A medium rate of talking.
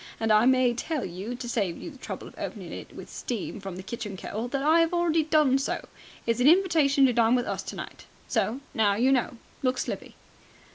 No: fast, 220 wpm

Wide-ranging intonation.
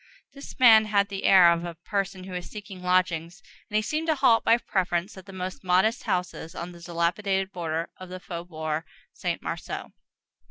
No: average, 2.8 semitones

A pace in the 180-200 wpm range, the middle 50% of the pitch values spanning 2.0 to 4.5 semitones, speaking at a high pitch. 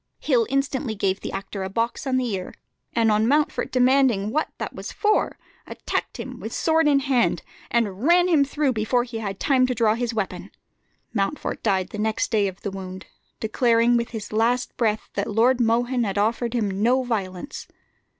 Yes: average, 185 wpm; average, 3.6 semitones; high, 230 Hz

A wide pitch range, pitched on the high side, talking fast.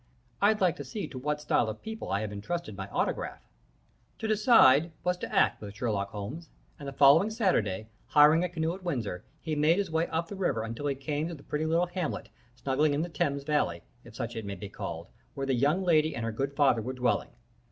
No: wide, 6.6 semitones; medium, 145 Hz; fast, 225 wpm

